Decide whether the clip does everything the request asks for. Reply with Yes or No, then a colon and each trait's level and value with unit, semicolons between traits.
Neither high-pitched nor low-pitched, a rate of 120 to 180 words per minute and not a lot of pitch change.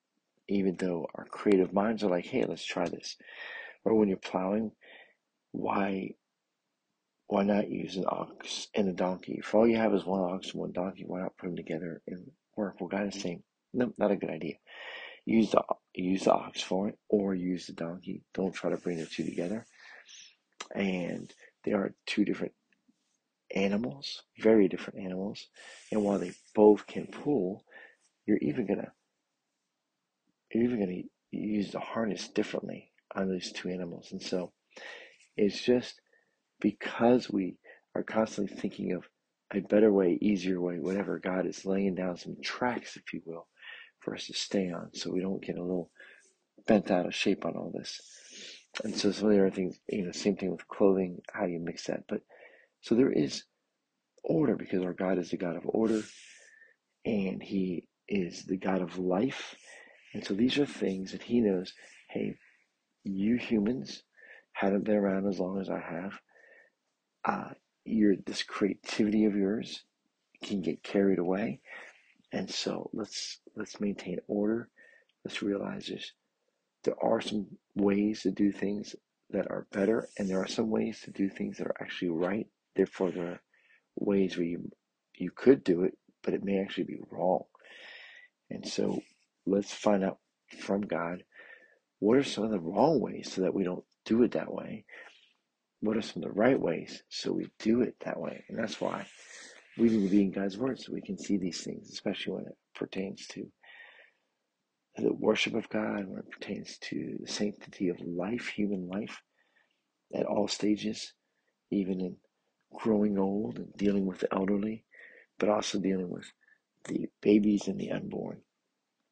No: low, 100 Hz; average, 175 wpm; narrow, 2.3 semitones